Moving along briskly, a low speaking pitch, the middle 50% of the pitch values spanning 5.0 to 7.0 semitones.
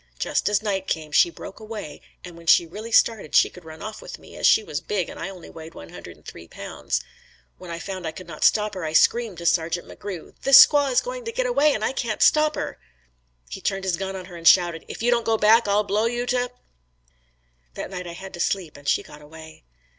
No: fast, 255 wpm; high, 190 Hz; average, 5.3 semitones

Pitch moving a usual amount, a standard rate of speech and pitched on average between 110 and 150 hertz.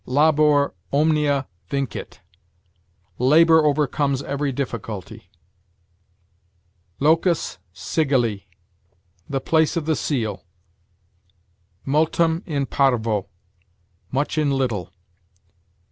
No: average, 3.0 semitones; slow, 75 wpm; medium, 140 Hz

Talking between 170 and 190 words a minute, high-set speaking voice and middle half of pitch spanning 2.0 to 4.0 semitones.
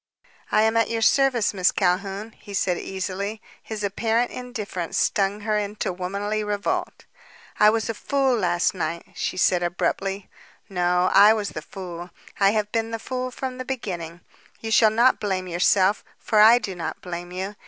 Yes: average, 175 wpm; high, 205 Hz; average, 3.4 semitones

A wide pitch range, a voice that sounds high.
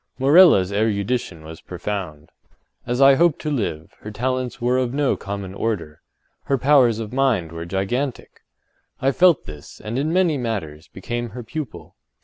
No: wide, 5.9 semitones; low, 115 Hz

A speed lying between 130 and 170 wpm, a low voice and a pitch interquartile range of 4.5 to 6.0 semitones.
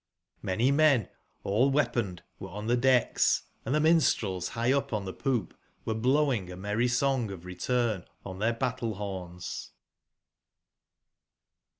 Yes: slow, 135 wpm; low, 115 Hz; average, 5.3 semitones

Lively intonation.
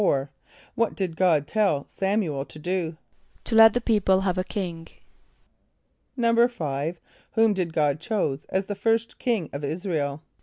Yes: wide, 5.7 semitones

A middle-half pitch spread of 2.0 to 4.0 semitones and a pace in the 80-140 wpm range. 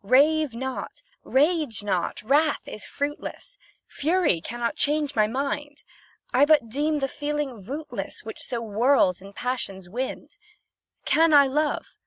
No: average, 4.4 semitones; slow, 135 wpm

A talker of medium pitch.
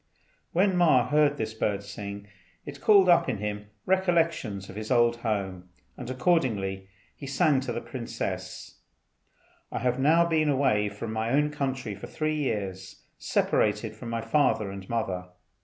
No: low, 120 Hz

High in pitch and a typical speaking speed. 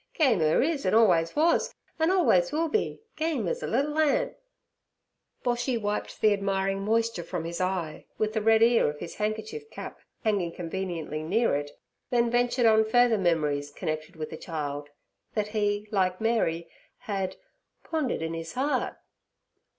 Yes: high, 210 Hz; average, 160 wpm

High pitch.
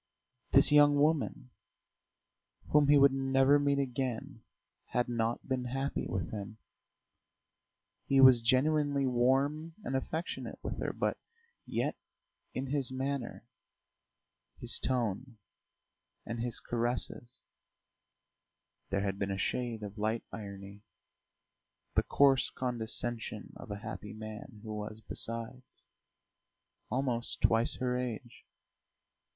No: low, 125 Hz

